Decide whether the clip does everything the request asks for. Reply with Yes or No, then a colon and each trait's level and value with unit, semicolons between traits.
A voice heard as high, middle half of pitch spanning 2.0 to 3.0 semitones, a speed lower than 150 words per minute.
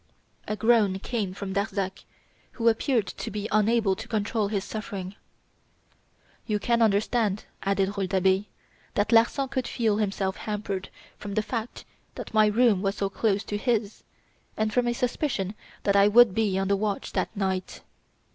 No: high, 210 Hz; narrow, 2.4 semitones; average, 160 wpm